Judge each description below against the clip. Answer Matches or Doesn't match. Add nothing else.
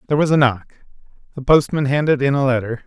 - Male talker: Matches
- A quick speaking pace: Matches